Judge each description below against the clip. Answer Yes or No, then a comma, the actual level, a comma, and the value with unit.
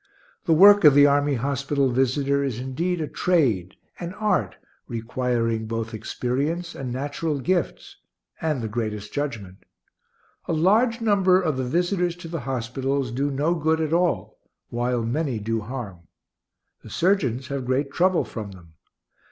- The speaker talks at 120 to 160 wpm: Yes, average, 150 wpm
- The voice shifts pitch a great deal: Yes, wide, 5.7 semitones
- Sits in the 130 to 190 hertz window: Yes, medium, 140 Hz